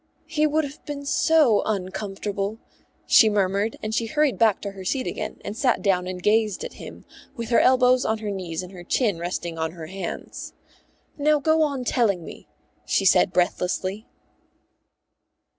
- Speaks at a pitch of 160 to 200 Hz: No, high, 215 Hz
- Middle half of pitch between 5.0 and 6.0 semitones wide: Yes, average, 5.3 semitones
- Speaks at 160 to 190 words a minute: Yes, average, 170 wpm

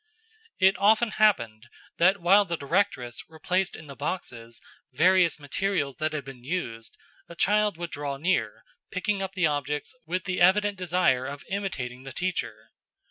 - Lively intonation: Yes, wide, 5.7 semitones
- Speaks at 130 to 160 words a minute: Yes, average, 155 wpm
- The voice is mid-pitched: Yes, medium, 170 Hz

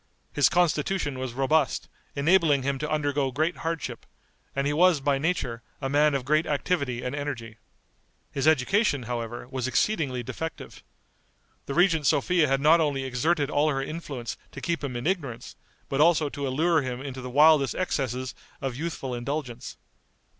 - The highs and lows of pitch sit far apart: No, average, 3.5 semitones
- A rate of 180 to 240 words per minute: No, average, 160 wpm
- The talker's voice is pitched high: No, medium, 140 Hz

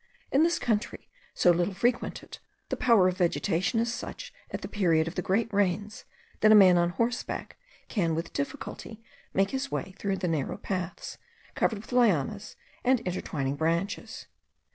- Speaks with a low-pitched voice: No, high, 195 Hz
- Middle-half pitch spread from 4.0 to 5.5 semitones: Yes, average, 4.8 semitones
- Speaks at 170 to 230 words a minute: No, average, 160 wpm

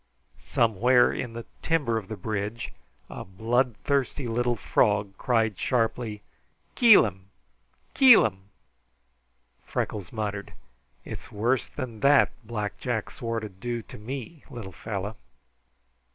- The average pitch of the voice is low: Yes, low, 115 Hz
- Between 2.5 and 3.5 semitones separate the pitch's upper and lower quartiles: Yes, average, 2.9 semitones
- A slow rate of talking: Yes, slow, 110 wpm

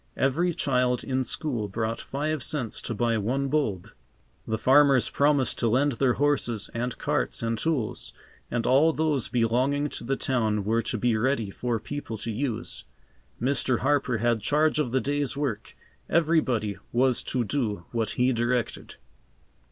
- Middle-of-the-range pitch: No, low, 125 Hz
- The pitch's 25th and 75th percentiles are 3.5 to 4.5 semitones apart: Yes, average, 3.8 semitones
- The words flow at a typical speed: Yes, average, 160 wpm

